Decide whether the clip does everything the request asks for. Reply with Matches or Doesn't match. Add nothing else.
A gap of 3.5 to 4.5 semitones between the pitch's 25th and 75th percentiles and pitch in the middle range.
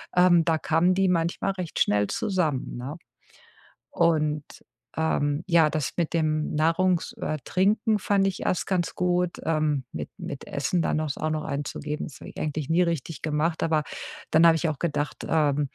Doesn't match